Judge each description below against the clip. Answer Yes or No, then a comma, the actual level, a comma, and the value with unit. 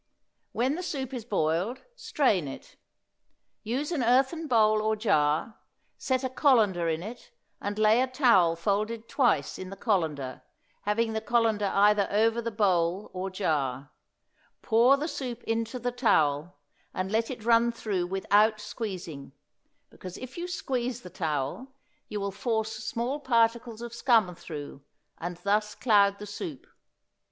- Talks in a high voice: Yes, high, 215 Hz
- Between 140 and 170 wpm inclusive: Yes, average, 150 wpm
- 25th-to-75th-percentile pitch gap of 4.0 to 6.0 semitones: Yes, average, 4.5 semitones